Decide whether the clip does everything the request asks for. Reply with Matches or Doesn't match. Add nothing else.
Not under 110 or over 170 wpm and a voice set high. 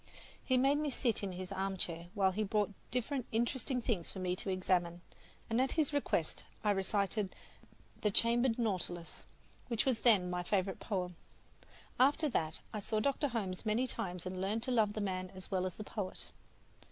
Doesn't match